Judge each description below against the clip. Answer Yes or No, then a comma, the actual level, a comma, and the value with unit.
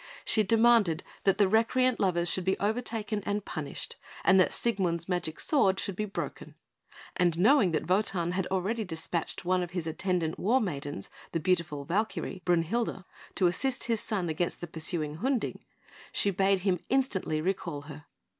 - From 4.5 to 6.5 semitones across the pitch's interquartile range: No, average, 3.9 semitones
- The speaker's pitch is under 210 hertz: Yes, medium, 185 Hz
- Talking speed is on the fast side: No, average, 165 wpm